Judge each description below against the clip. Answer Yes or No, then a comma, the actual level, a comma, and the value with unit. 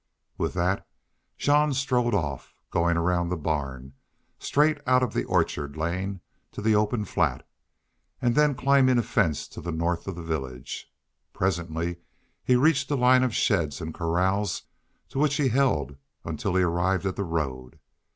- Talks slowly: No, average, 160 wpm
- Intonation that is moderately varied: No, wide, 7.4 semitones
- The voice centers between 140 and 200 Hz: No, very low, 95 Hz